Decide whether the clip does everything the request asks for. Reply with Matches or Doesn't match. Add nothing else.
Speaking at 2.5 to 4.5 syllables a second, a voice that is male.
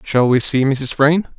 Matches